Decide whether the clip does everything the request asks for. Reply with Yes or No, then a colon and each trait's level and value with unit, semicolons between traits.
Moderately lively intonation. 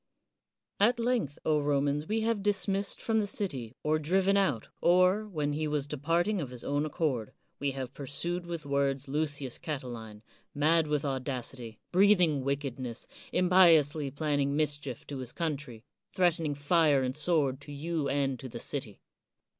Yes: average, 4.0 semitones